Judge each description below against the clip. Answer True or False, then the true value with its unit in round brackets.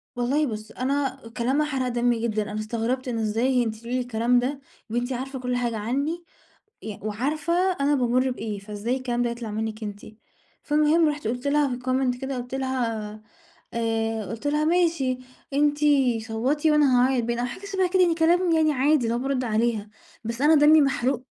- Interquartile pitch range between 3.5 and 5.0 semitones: True (3.8 semitones)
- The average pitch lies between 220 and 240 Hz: False (250 Hz)